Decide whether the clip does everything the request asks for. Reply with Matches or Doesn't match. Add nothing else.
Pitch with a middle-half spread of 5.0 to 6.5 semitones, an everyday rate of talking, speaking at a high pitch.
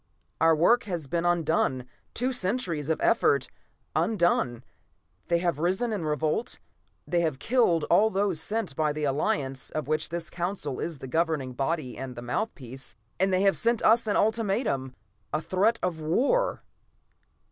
Doesn't match